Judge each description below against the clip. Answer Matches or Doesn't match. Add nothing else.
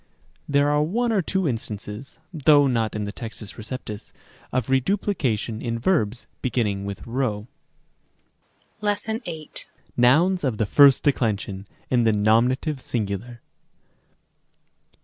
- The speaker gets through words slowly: Matches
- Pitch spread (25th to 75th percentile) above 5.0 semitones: Matches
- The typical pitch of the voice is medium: Doesn't match